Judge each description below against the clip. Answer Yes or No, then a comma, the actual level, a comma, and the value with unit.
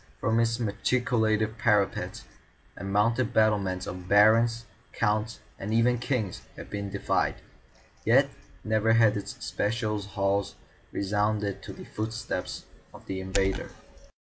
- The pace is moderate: No, slow, 120 wpm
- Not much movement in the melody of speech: Yes, narrow, 2.3 semitones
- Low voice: Yes, low, 105 Hz